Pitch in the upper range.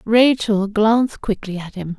Yes: high, 210 Hz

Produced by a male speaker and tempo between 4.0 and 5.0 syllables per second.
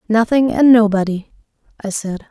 No: female; 4.7 syllables/s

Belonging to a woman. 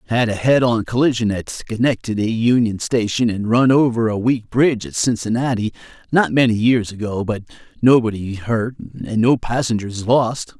No: male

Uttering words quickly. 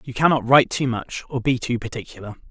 Yes: fast, 215 wpm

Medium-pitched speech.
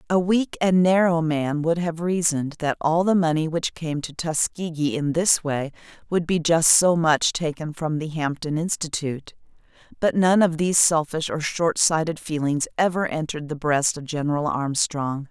Yes: medium, 160 Hz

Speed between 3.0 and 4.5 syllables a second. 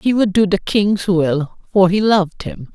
Yes: 4.2 syllables/s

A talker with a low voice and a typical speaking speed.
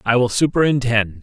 Yes: low, 120 Hz; average, 145 wpm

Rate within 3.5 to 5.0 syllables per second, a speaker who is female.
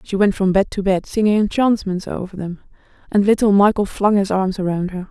No: 5.3 syllables/s; female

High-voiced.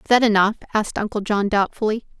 Yes: high, 210 Hz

